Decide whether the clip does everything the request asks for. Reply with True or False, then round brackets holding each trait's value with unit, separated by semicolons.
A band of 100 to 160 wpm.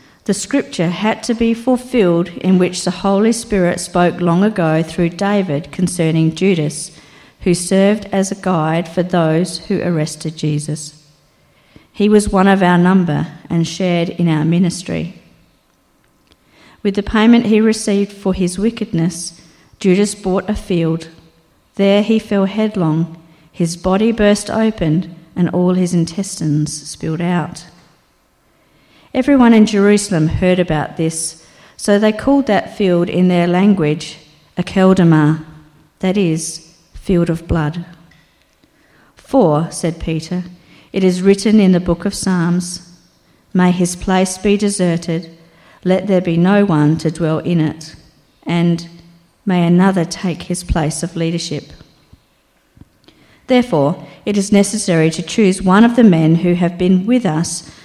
True (140 wpm)